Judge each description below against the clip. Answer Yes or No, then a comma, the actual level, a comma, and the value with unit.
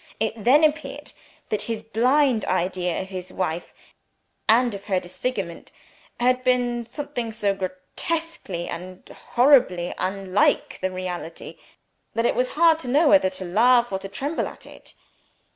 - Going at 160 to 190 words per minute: No, average, 145 wpm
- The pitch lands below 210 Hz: No, high, 220 Hz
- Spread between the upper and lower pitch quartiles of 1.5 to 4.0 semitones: No, wide, 5.4 semitones